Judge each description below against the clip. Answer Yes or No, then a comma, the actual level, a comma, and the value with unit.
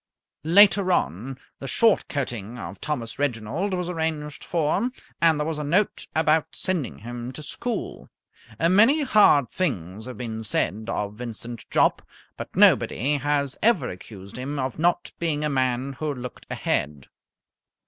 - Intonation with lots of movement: Yes, wide, 5.9 semitones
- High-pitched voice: No, medium, 140 Hz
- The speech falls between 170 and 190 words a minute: No, average, 150 wpm